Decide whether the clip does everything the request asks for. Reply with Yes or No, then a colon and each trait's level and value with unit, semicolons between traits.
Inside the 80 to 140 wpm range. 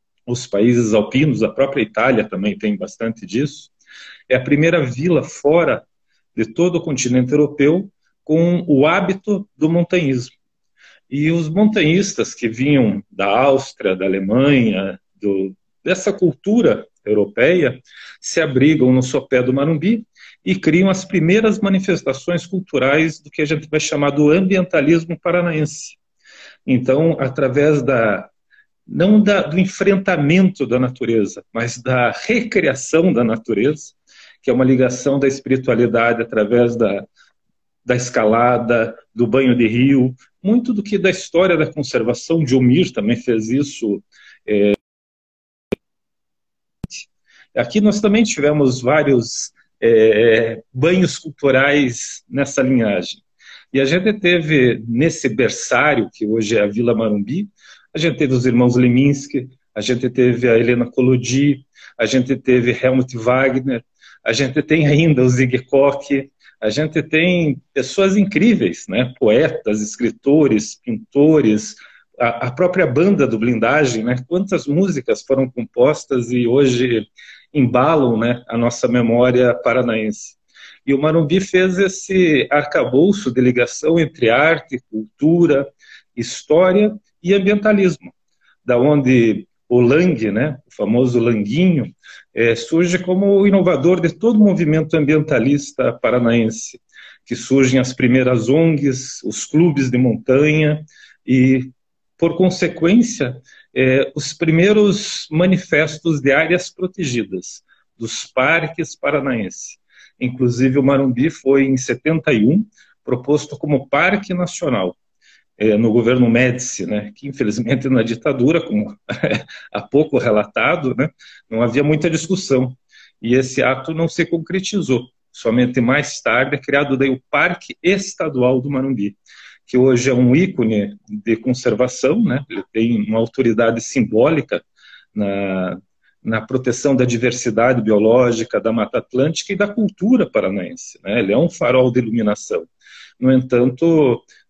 Yes: average, 125 wpm